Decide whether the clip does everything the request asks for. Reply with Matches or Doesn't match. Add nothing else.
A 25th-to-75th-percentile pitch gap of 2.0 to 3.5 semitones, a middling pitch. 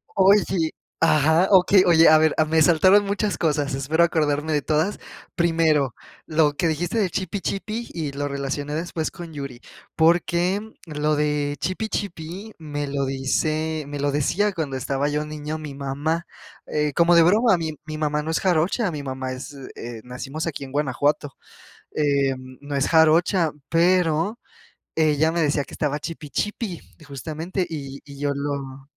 Matches